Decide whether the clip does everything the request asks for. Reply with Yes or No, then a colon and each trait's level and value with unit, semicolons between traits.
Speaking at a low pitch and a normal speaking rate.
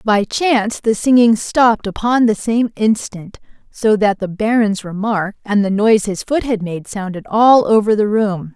No: high, 215 Hz; average, 180 wpm